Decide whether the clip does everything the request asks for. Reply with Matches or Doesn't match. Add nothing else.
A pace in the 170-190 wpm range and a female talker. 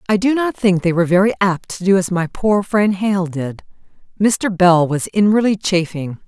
Doesn't match